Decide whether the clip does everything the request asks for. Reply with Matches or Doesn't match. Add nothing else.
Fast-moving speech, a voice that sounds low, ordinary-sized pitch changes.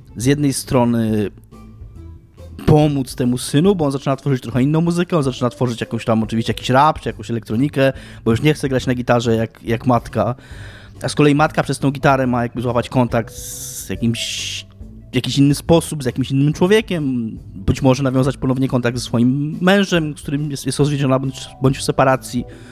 Matches